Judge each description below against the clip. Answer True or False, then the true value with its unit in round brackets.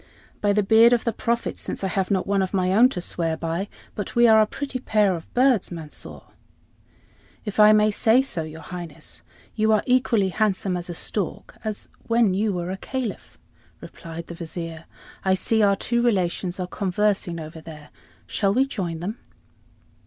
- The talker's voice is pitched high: True (195 Hz)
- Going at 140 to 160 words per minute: False (185 wpm)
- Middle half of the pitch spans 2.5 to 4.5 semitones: True (4.1 semitones)